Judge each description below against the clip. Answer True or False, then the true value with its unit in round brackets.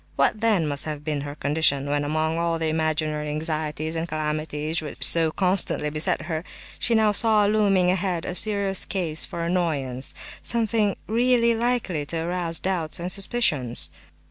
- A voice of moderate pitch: True (165 Hz)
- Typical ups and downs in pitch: True (4.3 semitones)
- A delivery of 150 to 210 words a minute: True (155 wpm)